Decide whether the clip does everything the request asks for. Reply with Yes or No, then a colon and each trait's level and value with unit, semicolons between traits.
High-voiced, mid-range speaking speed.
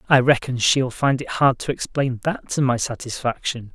No: low, 130 Hz; average, 190 wpm